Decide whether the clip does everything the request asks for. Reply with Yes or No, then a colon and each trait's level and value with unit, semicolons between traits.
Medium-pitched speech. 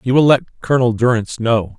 No: low, 120 Hz